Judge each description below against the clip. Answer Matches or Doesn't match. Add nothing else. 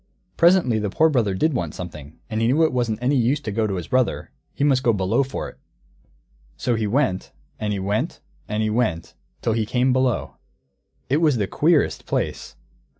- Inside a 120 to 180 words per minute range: Doesn't match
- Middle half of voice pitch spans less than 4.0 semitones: Doesn't match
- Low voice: Matches